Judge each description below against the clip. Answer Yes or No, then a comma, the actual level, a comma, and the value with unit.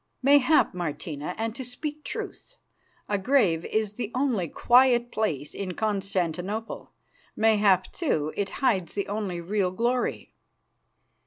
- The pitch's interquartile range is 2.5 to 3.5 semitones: No, average, 5.2 semitones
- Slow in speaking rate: Yes, slow, 120 wpm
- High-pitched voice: Yes, high, 210 Hz